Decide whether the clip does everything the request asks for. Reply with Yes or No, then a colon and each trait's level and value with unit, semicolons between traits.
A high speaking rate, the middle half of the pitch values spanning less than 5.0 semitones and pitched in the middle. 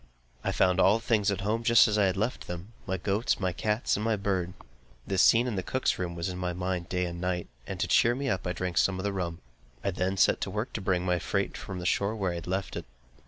No: fast, 270 wpm; average, 2.8 semitones; very low, 95 Hz